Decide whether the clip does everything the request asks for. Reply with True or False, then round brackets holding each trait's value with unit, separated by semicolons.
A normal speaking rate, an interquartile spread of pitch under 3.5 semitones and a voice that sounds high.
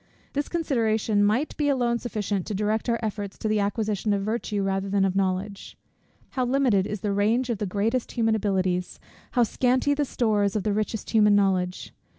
True (185 wpm; 3.0 semitones; 210 Hz)